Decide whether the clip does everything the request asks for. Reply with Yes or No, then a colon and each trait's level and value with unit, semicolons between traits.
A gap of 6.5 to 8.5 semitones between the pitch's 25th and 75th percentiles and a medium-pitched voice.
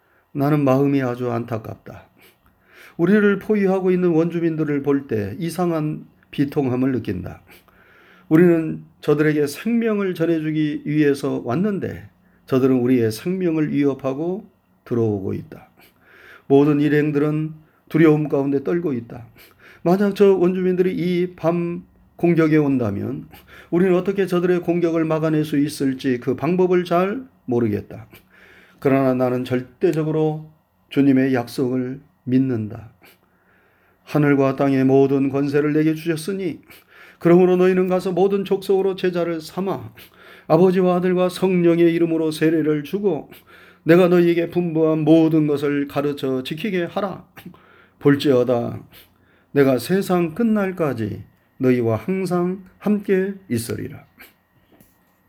No: wide, 5.4 semitones; medium, 155 Hz